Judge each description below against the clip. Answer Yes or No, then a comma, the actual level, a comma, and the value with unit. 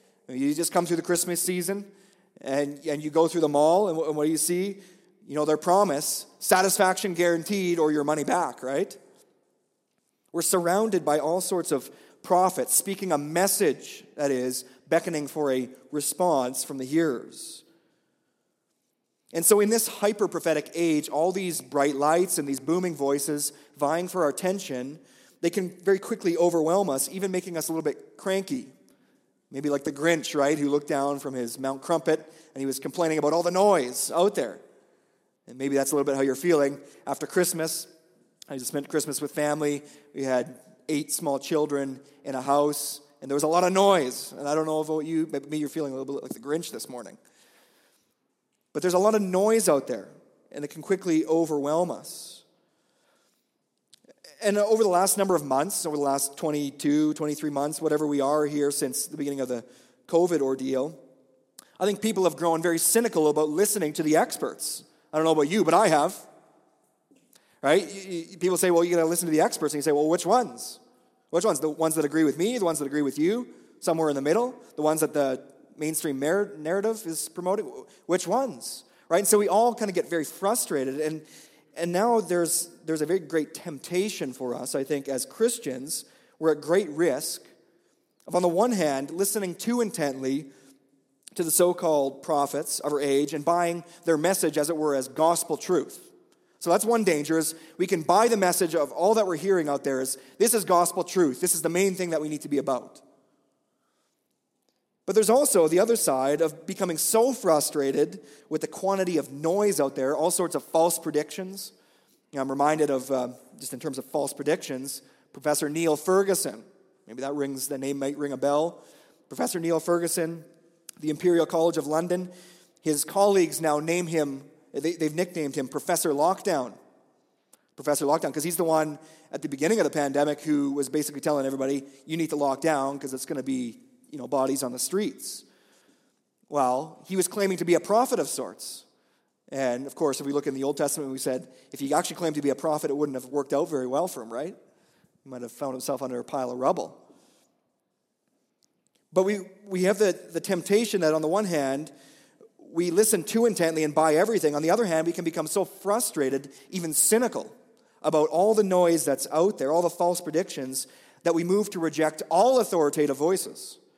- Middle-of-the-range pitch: Yes, medium, 160 Hz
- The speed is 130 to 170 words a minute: No, average, 195 wpm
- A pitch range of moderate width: Yes, average, 4.1 semitones